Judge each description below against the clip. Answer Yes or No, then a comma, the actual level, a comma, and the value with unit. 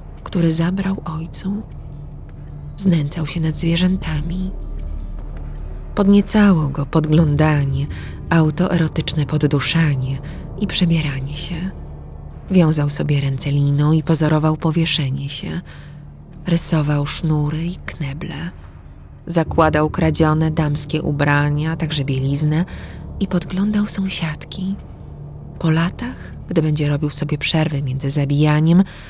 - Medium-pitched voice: Yes, medium, 155 Hz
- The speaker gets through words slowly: Yes, slow, 95 wpm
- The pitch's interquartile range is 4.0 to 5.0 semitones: No, average, 2.7 semitones